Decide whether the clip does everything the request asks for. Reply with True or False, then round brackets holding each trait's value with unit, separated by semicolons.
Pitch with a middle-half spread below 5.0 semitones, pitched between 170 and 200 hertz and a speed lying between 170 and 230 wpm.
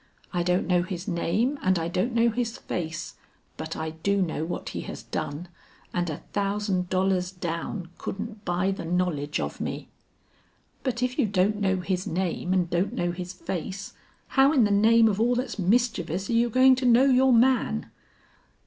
True (4.6 semitones; 190 Hz; 185 wpm)